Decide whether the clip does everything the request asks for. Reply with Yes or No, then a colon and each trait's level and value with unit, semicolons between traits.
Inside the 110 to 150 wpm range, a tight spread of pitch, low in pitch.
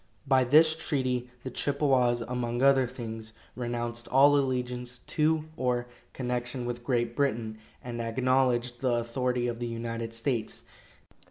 Yes: slow, 135 wpm; narrow, 1.7 semitones; low, 125 Hz